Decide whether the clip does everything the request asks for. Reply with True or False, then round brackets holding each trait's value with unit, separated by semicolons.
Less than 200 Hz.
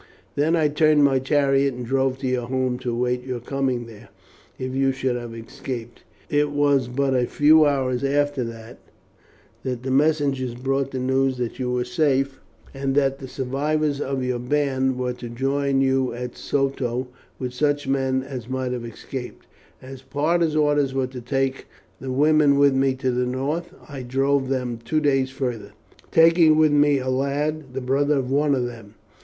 True (135 Hz)